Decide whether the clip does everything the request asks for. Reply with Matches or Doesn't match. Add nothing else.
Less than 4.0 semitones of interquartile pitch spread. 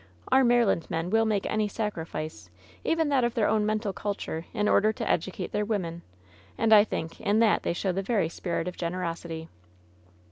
Doesn't match